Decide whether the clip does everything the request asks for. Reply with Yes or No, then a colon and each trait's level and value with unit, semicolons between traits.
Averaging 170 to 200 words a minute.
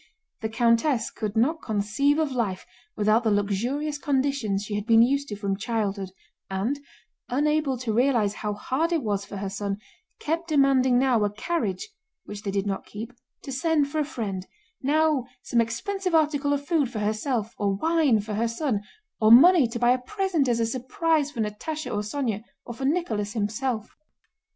Yes: average, 180 wpm